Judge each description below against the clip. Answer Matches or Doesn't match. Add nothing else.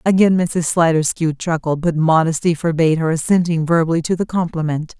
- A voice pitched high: Doesn't match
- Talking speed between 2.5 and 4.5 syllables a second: Doesn't match